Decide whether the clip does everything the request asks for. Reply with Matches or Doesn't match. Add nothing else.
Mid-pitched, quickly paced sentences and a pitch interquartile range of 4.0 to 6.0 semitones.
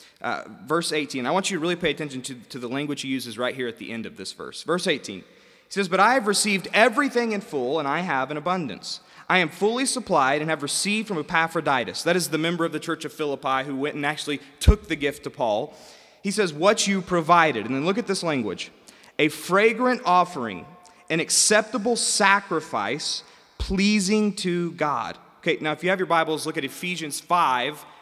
Matches